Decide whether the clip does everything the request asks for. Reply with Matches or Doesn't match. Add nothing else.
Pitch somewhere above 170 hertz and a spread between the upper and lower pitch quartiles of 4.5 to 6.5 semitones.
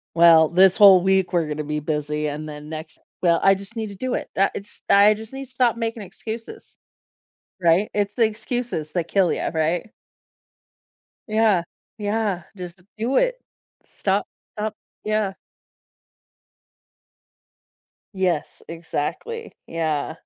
Matches